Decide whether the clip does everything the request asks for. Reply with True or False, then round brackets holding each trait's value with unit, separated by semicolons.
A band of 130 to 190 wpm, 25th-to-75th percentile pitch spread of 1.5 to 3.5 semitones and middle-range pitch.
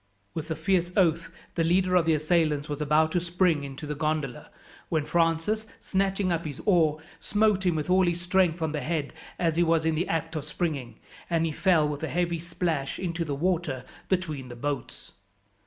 False (200 wpm; 2.7 semitones; 165 Hz)